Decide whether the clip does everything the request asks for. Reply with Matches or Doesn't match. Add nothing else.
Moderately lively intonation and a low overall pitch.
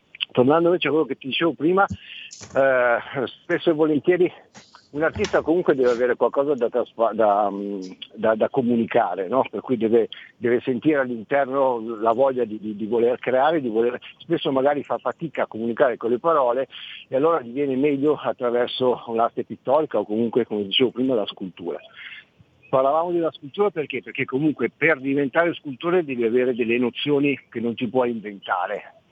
Matches